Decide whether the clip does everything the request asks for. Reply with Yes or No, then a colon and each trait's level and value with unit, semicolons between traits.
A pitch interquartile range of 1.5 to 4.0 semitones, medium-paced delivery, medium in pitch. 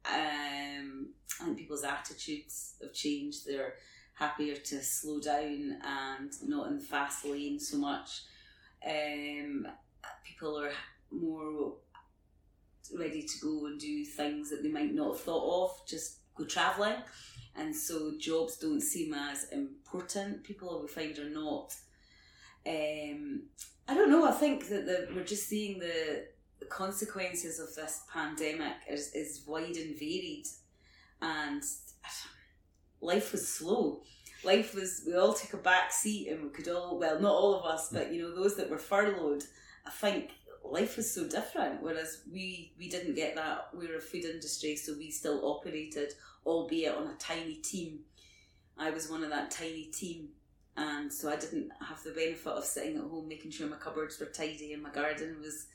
No: average, 4.9 semitones; average, 170 wpm; medium, 160 Hz